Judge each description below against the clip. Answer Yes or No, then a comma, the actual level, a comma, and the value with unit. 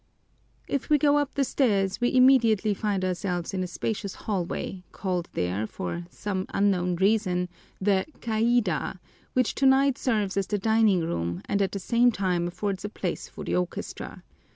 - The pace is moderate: Yes, average, 165 wpm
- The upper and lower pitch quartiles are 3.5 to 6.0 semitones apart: Yes, average, 4.1 semitones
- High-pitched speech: Yes, high, 200 Hz